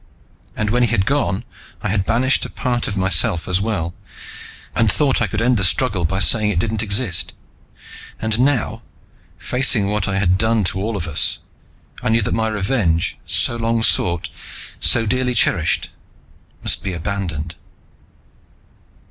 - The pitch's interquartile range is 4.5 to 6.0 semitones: No, average, 3.7 semitones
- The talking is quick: No, average, 160 wpm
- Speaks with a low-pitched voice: Yes, low, 105 Hz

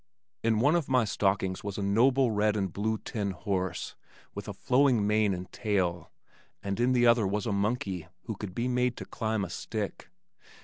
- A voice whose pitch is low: Yes, low, 105 Hz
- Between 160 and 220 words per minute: Yes, average, 190 wpm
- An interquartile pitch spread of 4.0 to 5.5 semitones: No, average, 3.5 semitones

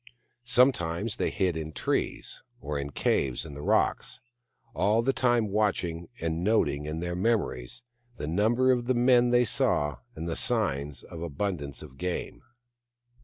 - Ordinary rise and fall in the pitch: No, wide, 7.4 semitones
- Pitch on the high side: No, very low, 90 Hz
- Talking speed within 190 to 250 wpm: No, average, 160 wpm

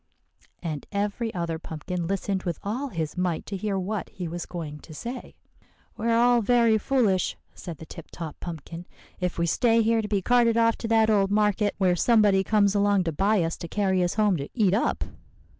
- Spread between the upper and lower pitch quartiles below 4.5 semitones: Yes, average, 4.1 semitones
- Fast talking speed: Yes, fast, 210 wpm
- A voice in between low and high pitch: No, high, 200 Hz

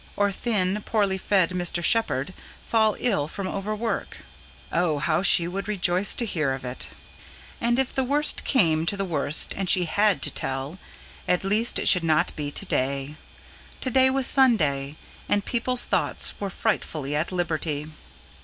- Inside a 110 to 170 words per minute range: Yes, average, 165 wpm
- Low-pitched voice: No, medium, 185 Hz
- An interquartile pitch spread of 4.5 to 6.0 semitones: Yes, wide, 5.6 semitones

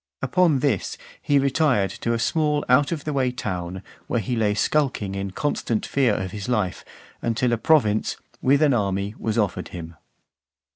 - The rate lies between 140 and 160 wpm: No, average, 175 wpm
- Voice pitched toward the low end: Yes, low, 120 Hz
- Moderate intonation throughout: No, wide, 5.8 semitones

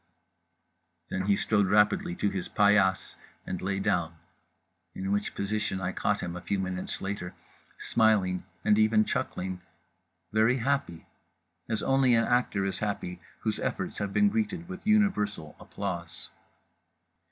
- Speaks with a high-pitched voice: No, low, 100 Hz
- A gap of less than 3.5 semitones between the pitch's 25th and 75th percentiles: Yes, average, 3.0 semitones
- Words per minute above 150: No, average, 140 wpm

